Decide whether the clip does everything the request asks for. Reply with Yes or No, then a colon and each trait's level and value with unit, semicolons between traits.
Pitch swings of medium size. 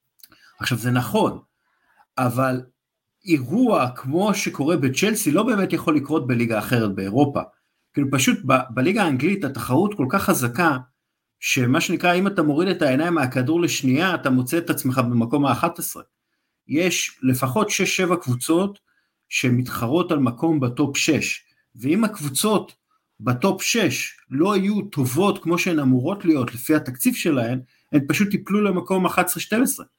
No: wide, 6.3 semitones